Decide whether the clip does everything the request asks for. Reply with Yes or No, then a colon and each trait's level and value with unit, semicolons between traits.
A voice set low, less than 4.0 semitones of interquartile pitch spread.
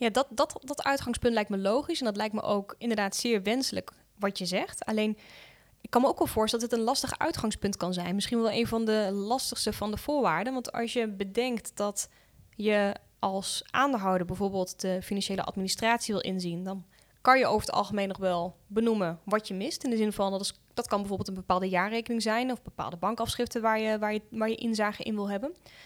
No: high, 215 Hz; average, 3.2 semitones